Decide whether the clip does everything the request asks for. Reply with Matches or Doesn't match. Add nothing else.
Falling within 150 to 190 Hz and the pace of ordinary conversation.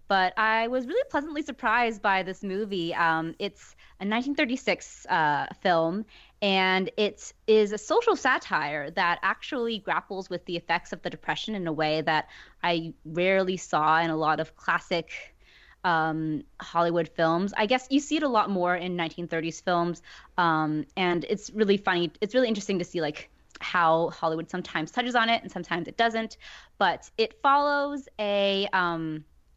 Matches